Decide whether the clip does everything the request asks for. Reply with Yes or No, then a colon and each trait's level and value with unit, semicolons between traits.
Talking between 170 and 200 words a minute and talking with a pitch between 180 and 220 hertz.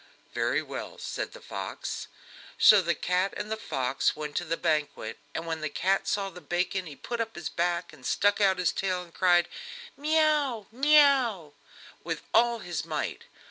Yes: average, 185 wpm; medium, 185 Hz